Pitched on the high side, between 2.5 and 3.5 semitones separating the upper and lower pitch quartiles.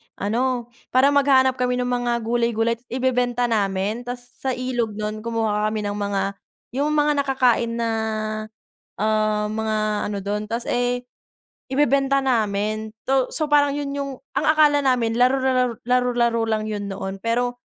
Yes: high, 240 Hz; average, 3.2 semitones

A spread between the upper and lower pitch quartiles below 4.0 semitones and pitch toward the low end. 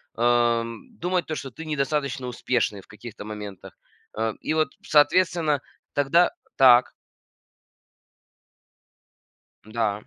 No: average, 5.1 semitones; low, 125 Hz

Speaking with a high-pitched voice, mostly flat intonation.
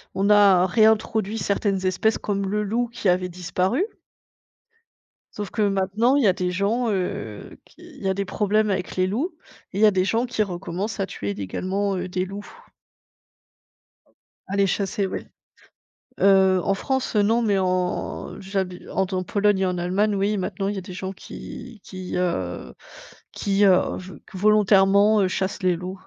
Yes: high, 195 Hz; narrow, 2.1 semitones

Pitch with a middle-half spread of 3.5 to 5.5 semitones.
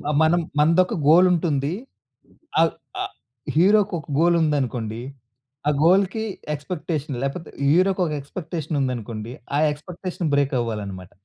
Yes: average, 4.6 semitones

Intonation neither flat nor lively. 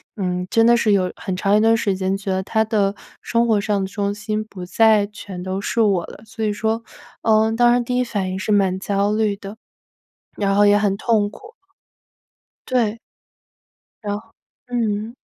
No: narrow, 2.1 semitones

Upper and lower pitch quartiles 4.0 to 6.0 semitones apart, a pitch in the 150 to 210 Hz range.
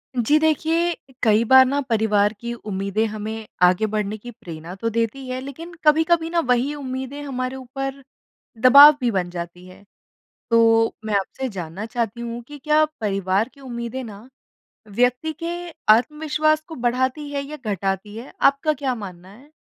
No: average, 4.8 semitones; high, 240 Hz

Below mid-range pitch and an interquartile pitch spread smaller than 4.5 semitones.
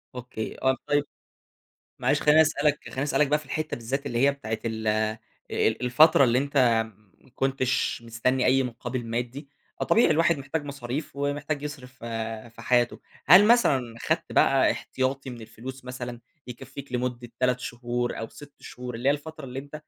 Yes: low, 130 Hz; average, 2.9 semitones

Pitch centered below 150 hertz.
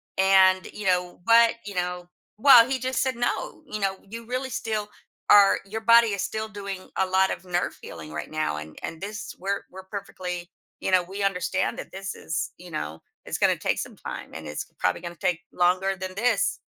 No: high, 190 Hz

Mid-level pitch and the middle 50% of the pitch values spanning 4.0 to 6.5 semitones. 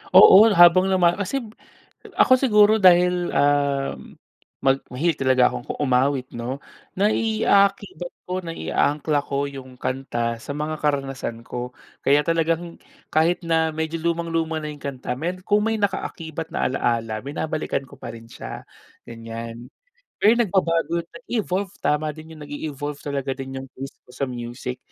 Yes: medium, 150 Hz; average, 4.7 semitones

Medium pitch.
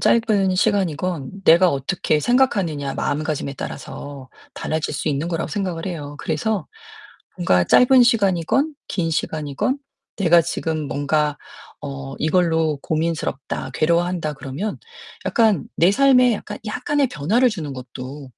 Yes: medium, 165 Hz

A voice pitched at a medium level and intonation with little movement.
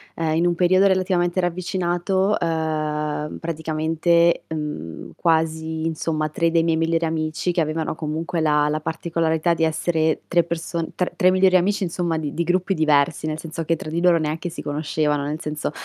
Yes: medium, 165 Hz; narrow, 1.9 semitones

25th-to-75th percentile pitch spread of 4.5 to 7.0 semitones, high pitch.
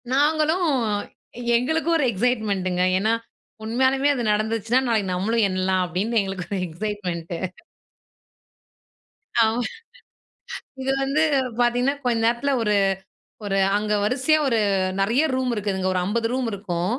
Yes: average, 4.8 semitones; high, 225 Hz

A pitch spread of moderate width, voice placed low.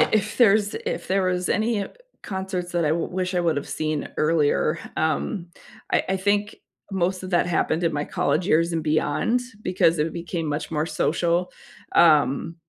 No: average, 3.2 semitones; medium, 175 Hz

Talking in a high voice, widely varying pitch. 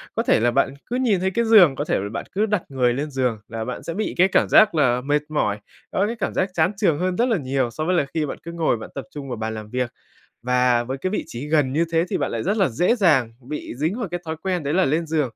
No: medium, 150 Hz; wide, 6.6 semitones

